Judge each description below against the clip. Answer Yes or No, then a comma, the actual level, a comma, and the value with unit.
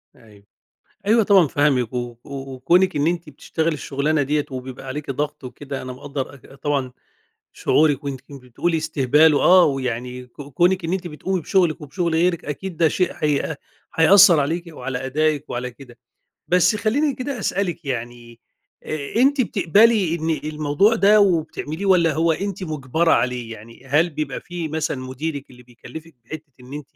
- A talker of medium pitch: Yes, medium, 150 Hz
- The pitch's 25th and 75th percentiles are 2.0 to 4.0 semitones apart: No, average, 4.7 semitones